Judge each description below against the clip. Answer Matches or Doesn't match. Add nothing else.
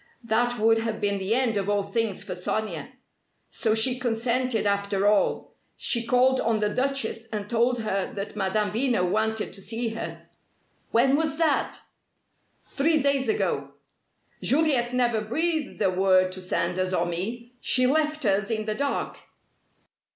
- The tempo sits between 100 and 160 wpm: Matches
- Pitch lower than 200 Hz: Doesn't match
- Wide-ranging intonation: Doesn't match